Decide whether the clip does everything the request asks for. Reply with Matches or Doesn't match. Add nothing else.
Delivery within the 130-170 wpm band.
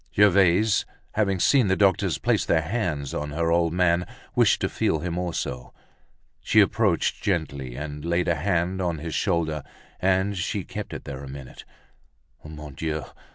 Matches